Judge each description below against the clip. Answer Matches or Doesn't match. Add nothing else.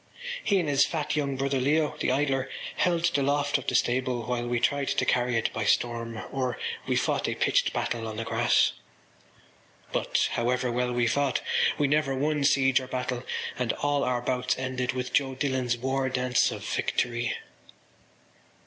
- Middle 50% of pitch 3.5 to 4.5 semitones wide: Doesn't match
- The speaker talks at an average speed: Matches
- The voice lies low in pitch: Matches